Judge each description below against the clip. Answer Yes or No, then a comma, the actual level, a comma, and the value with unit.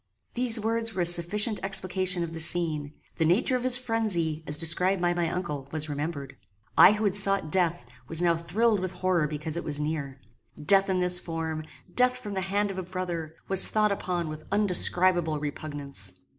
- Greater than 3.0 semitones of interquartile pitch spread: Yes, average, 3.9 semitones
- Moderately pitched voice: Yes, medium, 175 Hz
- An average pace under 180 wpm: No, average, 190 wpm